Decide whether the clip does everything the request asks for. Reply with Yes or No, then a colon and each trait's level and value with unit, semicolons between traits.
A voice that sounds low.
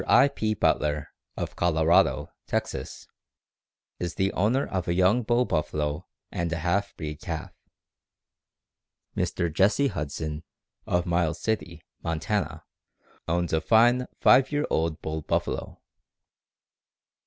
Yes: very low, 85 Hz